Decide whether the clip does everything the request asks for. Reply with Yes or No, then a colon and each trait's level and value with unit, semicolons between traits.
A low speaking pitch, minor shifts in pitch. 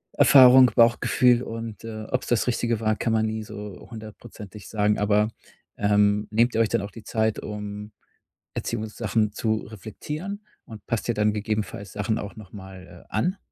Yes: low, 110 Hz; narrow, 1.8 semitones